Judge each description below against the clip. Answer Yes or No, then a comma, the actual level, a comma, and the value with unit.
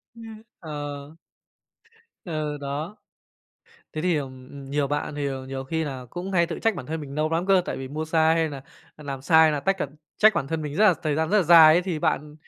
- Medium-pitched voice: Yes, medium, 155 Hz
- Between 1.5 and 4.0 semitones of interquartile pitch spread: Yes, average, 3.0 semitones